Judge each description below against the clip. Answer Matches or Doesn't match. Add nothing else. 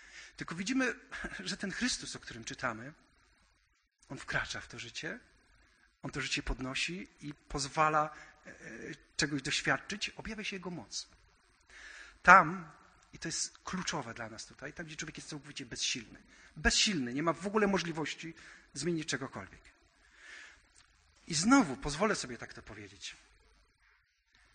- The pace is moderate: Matches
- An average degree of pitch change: Doesn't match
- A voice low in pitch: Doesn't match